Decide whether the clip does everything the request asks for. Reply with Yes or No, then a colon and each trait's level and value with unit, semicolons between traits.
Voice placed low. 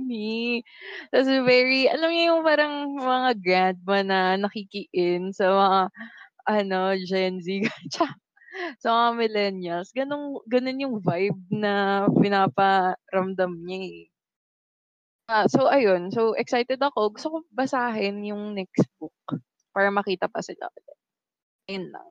No: high, 205 Hz